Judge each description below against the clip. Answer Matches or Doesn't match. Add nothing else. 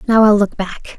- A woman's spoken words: Matches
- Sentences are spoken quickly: Matches